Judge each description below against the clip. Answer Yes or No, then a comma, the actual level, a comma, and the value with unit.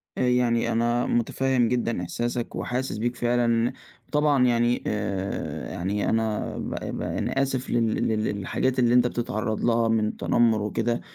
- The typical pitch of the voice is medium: No, low, 120 Hz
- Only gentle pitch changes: Yes, narrow, 2.0 semitones